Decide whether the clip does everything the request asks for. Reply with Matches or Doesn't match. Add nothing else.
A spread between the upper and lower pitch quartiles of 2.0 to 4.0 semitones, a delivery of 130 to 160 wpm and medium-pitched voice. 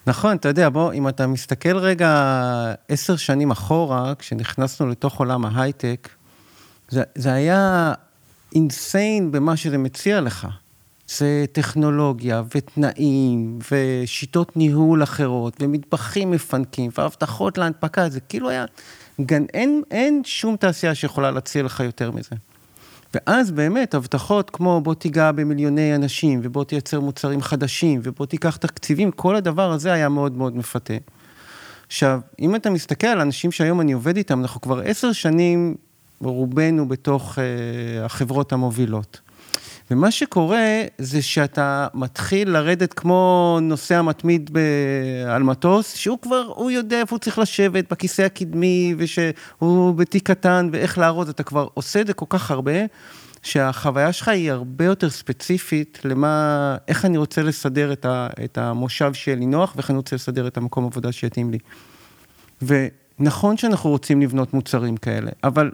Doesn't match